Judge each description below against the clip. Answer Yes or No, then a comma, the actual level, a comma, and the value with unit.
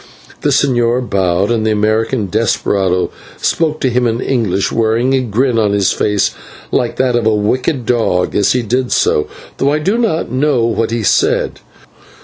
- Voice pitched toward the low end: Yes, low, 115 Hz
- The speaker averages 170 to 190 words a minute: Yes, average, 175 wpm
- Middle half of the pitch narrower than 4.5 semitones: Yes, average, 3.6 semitones